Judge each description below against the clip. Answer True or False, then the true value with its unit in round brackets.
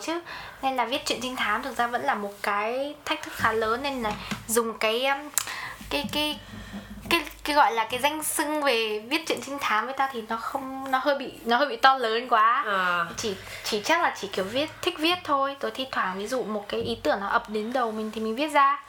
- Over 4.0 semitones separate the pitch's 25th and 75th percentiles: True (4.6 semitones)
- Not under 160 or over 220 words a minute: False (245 wpm)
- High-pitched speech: True (260 Hz)